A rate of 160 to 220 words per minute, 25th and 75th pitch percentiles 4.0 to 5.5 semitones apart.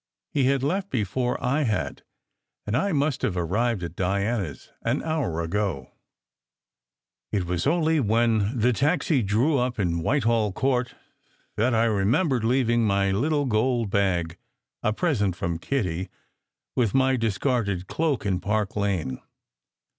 No: average, 140 wpm; average, 5.1 semitones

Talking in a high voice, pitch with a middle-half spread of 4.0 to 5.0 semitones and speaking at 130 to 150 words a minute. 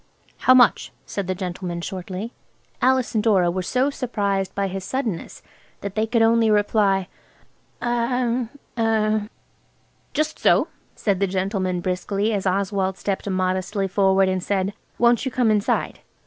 No: high, 200 Hz; average, 3.5 semitones; average, 140 wpm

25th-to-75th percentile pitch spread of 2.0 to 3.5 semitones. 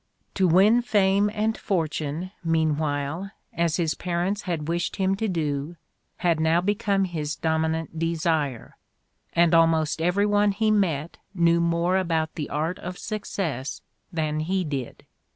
Yes: average, 3.2 semitones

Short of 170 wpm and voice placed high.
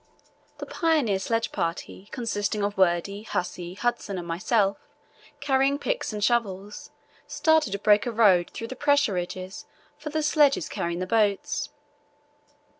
Yes: average, 140 wpm; high, 210 Hz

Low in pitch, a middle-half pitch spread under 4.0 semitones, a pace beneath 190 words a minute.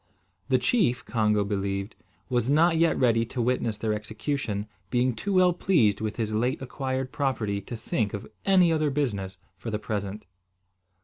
No: low, 120 Hz; average, 4.7 semitones; average, 165 wpm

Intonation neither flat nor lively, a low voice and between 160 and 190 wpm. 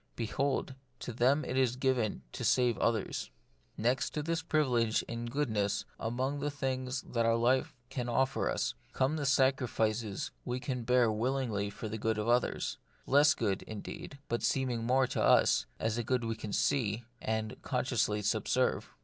Yes: average, 3.0 semitones; low, 125 Hz; average, 165 wpm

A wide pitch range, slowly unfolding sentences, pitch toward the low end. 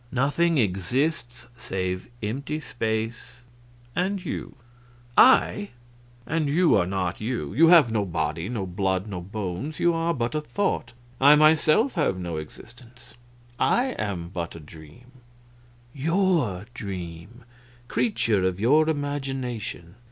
Yes: wide, 8.4 semitones; slow, 125 wpm; low, 120 Hz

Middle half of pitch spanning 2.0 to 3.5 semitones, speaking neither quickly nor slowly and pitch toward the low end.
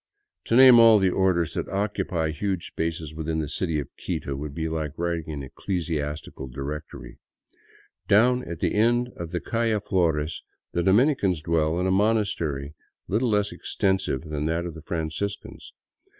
No: average, 4.6 semitones; average, 160 wpm; very low, 85 Hz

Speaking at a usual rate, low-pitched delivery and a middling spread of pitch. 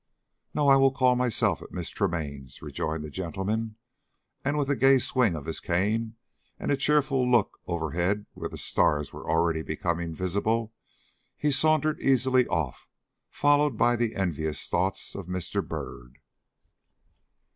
No: average, 145 wpm; low, 105 Hz; wide, 7.9 semitones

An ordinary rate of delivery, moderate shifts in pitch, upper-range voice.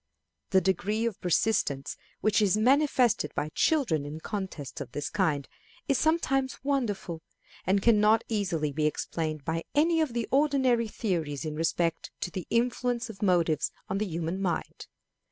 No: average, 155 wpm; wide, 6.5 semitones; high, 195 Hz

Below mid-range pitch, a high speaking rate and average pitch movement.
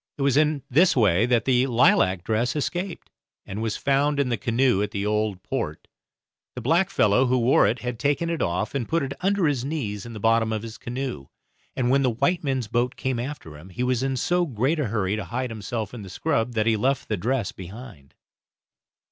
Yes: low, 120 Hz; fast, 215 wpm; average, 4.2 semitones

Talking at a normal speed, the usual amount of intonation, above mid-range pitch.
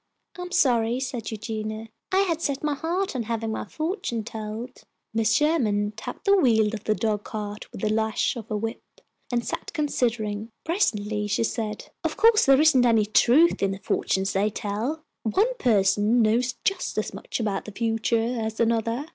Yes: average, 180 wpm; average, 3.9 semitones; high, 225 Hz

